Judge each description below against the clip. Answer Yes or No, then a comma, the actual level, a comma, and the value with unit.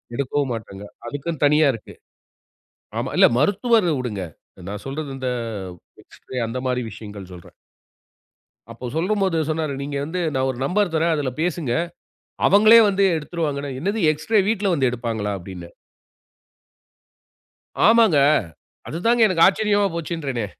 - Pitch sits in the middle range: Yes, medium, 150 Hz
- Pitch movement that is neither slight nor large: No, wide, 6.8 semitones